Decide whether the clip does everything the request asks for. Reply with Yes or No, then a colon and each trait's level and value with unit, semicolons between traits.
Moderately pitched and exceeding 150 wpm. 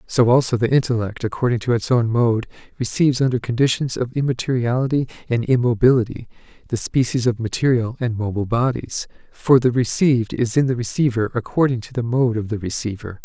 No: low, 120 Hz; average, 170 wpm